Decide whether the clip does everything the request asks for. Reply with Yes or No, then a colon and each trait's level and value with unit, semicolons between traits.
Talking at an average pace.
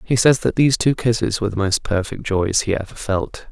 No: fast, 240 wpm